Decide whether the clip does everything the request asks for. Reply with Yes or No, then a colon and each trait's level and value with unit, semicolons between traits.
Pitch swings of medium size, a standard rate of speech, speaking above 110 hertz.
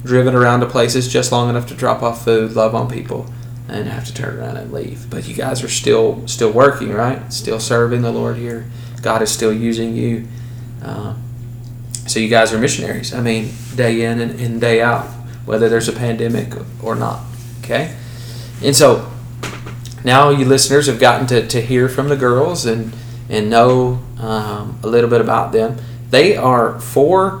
No: narrow, 1.1 semitones; average, 185 wpm; low, 120 Hz